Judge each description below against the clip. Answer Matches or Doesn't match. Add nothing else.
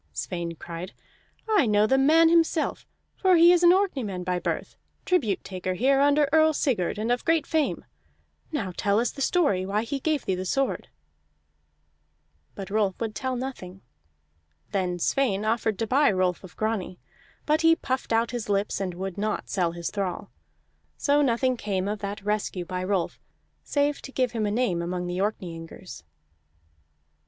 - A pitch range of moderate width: Doesn't match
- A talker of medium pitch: Doesn't match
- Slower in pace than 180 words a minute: Matches